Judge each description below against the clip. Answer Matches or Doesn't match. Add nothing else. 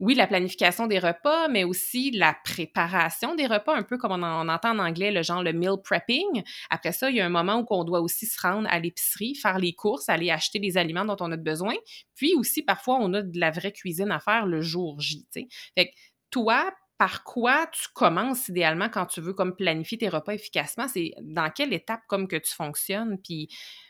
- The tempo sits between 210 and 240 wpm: Matches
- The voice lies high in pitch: Matches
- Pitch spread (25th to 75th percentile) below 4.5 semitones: Doesn't match